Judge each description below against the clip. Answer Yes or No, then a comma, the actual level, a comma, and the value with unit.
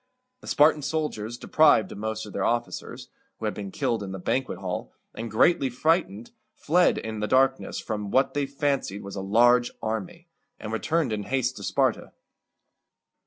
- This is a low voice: Yes, low, 120 Hz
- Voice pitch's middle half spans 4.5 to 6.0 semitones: Yes, average, 4.9 semitones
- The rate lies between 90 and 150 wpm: No, average, 170 wpm